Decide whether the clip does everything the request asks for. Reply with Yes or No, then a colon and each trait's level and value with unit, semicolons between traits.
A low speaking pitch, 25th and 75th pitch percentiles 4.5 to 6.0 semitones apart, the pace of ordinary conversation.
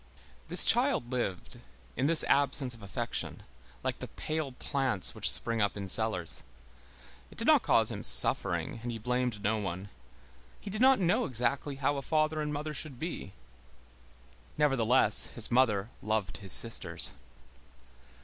Yes: low, 125 Hz; wide, 5.5 semitones; average, 150 wpm